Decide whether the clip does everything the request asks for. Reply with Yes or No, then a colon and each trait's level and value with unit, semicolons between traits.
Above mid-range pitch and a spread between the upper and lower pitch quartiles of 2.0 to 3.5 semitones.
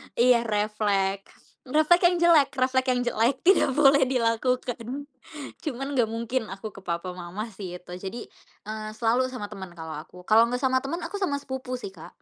No: high, 235 Hz; average, 4.7 semitones